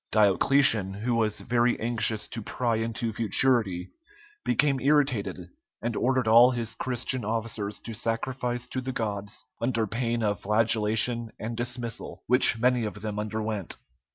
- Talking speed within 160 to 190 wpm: No, average, 140 wpm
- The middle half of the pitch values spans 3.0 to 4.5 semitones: No, narrow, 2.4 semitones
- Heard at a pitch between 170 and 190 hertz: No, low, 115 Hz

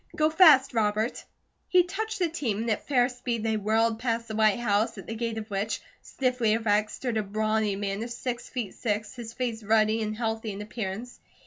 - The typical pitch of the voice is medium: No, high, 225 Hz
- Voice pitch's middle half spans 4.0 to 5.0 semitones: No, narrow, 2.4 semitones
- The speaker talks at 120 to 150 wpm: No, fast, 205 wpm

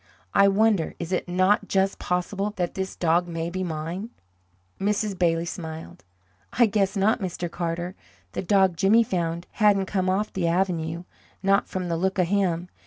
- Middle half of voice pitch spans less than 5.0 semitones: Yes, narrow, 2.5 semitones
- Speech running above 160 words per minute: Yes, average, 170 wpm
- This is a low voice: No, medium, 185 Hz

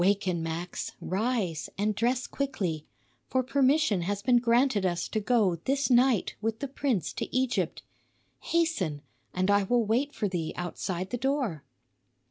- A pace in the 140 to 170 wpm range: Yes, average, 150 wpm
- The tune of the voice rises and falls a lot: Yes, wide, 5.9 semitones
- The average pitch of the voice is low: No, high, 215 Hz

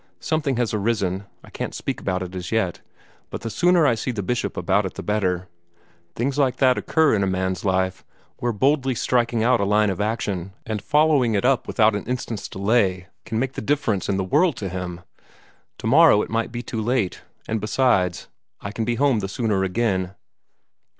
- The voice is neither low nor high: No, low, 110 Hz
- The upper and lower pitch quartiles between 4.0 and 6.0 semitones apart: Yes, average, 4.6 semitones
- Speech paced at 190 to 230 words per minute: Yes, average, 200 wpm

